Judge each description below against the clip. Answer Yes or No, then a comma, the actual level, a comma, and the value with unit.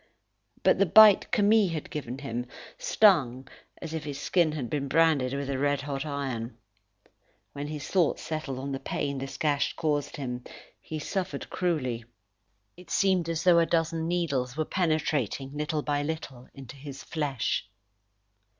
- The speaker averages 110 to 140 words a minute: No, average, 160 wpm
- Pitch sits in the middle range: Yes, medium, 145 Hz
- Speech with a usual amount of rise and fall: Yes, average, 3.4 semitones